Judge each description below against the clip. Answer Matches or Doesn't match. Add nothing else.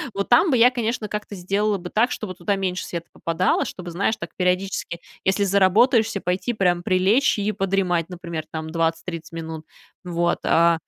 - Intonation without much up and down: Doesn't match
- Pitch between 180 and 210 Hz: Matches